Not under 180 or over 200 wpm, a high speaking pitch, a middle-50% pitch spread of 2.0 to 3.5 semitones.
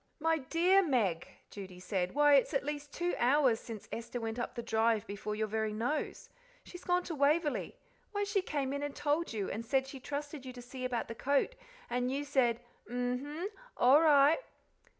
No: average, 195 wpm; very high, 270 Hz; average, 4.3 semitones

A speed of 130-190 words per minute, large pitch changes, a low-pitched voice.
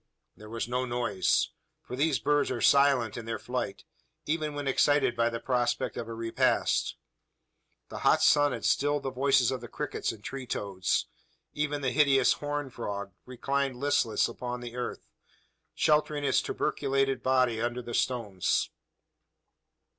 No: average, 155 wpm; average, 3.2 semitones; low, 125 Hz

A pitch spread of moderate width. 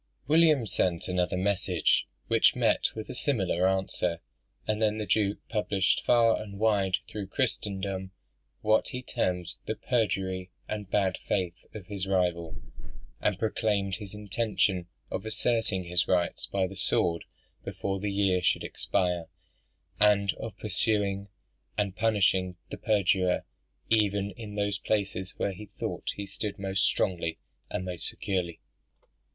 No: narrow, 2.3 semitones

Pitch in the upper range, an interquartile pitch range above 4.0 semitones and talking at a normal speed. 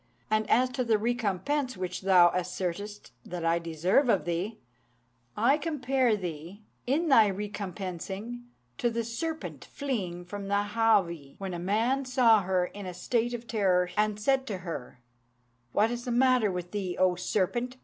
Yes: high, 205 Hz; average, 5.0 semitones; average, 160 wpm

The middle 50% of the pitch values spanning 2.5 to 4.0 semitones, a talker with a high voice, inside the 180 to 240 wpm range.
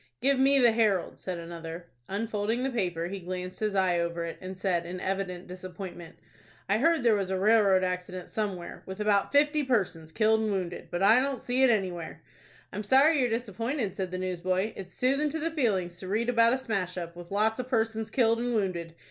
No: average, 4.4 semitones; high, 200 Hz; fast, 205 wpm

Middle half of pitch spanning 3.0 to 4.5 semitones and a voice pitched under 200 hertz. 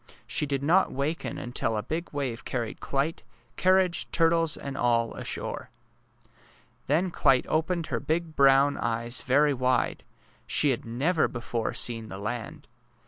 No: average, 5.3 semitones; medium, 140 Hz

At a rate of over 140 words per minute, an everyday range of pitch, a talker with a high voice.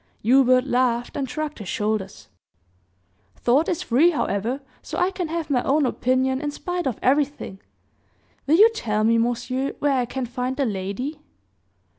Yes: average, 160 wpm; average, 3.6 semitones; very high, 260 Hz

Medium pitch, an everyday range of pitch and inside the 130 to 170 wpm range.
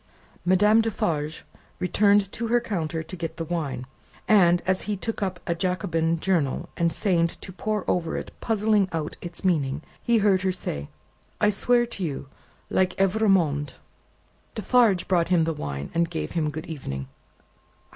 Yes: medium, 180 Hz; average, 3.9 semitones; average, 160 wpm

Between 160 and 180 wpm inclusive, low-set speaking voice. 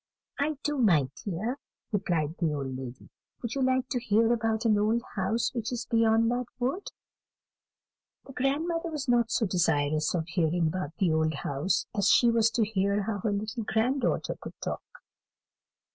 No: average, 175 wpm; high, 220 Hz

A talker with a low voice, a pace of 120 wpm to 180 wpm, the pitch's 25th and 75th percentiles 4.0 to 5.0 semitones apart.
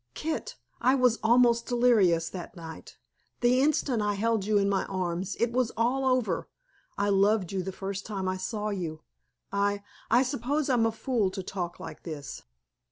No: high, 210 Hz; average, 175 wpm; average, 4.4 semitones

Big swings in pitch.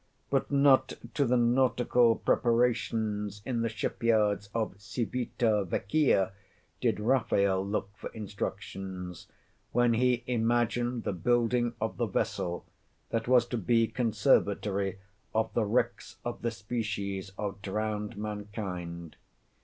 No: average, 3.1 semitones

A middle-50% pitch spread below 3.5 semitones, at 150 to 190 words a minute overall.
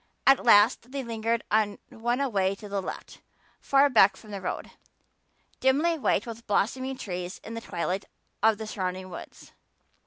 No: average, 4.2 semitones; average, 160 wpm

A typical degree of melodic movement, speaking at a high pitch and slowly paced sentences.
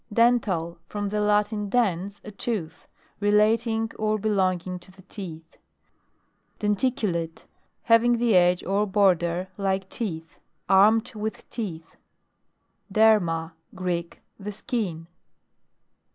Yes: average, 3.4 semitones; high, 200 Hz; slow, 105 wpm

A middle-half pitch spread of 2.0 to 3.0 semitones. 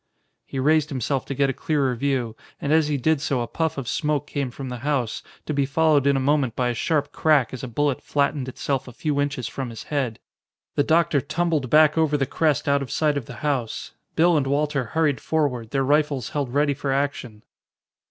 Yes: narrow, 2.5 semitones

